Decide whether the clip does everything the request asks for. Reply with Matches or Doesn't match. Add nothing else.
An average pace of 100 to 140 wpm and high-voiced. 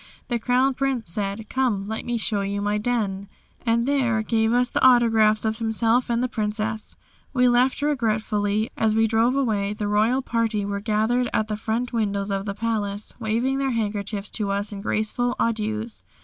Doesn't match